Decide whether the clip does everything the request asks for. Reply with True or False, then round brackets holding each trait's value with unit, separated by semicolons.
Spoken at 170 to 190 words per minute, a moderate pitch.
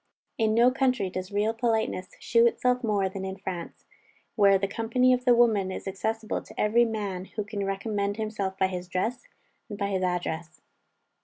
False (180 wpm; 205 Hz)